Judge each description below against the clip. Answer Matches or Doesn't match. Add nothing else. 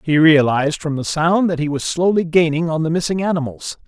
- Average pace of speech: Doesn't match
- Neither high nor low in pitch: Matches